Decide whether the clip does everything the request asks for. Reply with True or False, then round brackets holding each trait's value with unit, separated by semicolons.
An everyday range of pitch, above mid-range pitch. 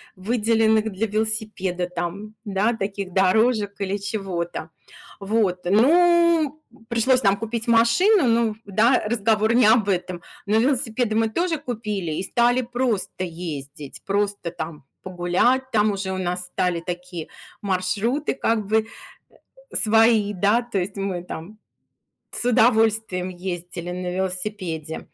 True (3.9 semitones; 210 Hz)